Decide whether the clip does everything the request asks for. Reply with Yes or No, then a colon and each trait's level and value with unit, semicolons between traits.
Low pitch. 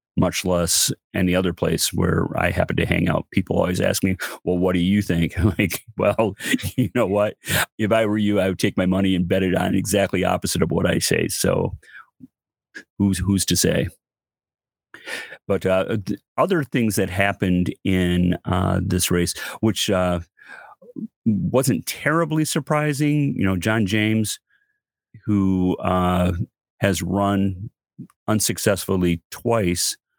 Yes: very low, 95 Hz